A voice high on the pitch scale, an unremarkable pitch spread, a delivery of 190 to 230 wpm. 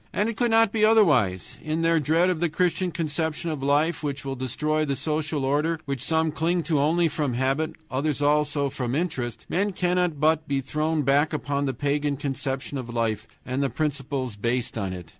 No: medium, 150 Hz; average, 3.2 semitones; average, 195 wpm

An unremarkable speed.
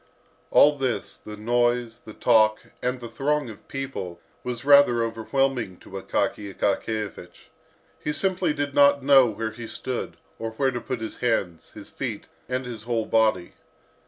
Yes: average, 160 wpm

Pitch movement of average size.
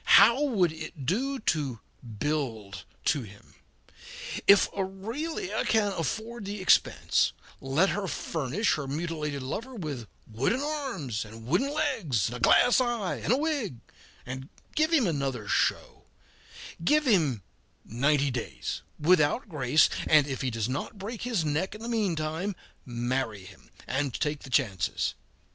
No: wide, 8.8 semitones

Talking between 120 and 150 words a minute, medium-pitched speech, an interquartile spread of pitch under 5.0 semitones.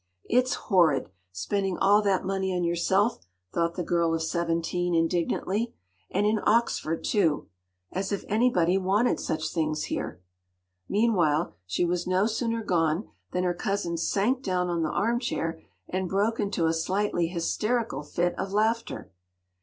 Yes: average, 140 wpm; medium, 180 Hz; average, 3.8 semitones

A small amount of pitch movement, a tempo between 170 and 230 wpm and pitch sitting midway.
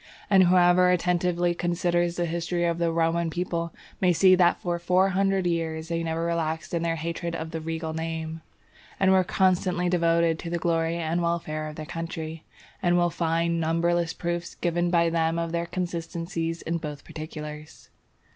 Yes: narrow, 1.2 semitones; average, 175 wpm; medium, 170 Hz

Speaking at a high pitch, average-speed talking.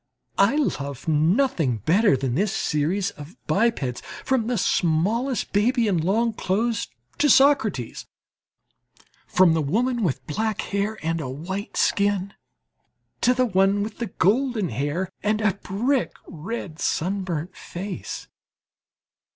No: high, 195 Hz; slow, 125 wpm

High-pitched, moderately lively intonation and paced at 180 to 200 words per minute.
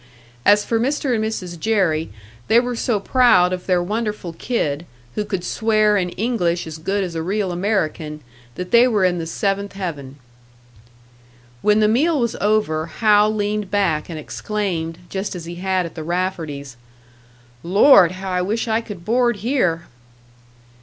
No: high, 195 Hz; average, 4.0 semitones; average, 165 wpm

